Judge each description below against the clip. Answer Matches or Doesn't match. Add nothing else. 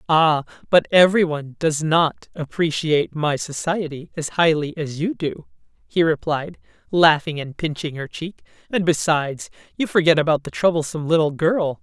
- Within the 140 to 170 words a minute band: Matches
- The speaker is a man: Doesn't match